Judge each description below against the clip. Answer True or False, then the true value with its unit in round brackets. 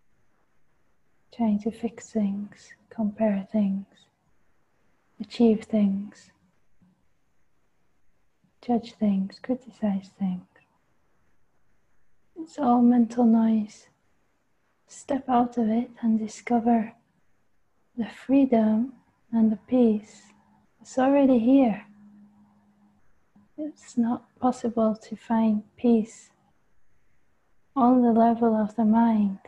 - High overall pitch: True (225 Hz)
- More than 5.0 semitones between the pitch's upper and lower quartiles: False (2.4 semitones)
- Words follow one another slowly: True (85 wpm)